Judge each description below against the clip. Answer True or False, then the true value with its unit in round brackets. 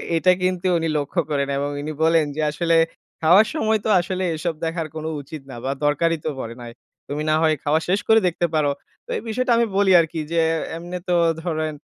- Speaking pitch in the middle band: True (165 Hz)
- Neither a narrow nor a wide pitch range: True (3.0 semitones)